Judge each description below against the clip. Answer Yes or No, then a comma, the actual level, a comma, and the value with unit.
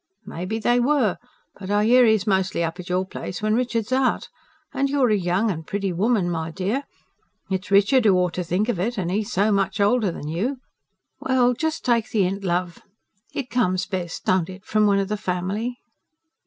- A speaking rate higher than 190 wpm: Yes, fast, 205 wpm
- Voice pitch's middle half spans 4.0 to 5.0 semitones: Yes, average, 4.3 semitones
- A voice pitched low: No, high, 200 Hz